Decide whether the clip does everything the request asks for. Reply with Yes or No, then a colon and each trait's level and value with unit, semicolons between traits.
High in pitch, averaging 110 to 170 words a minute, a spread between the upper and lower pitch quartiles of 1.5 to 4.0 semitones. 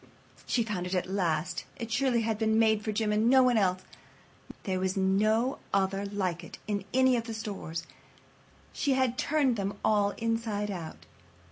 No: high, 210 Hz; average, 190 wpm; average, 3.3 semitones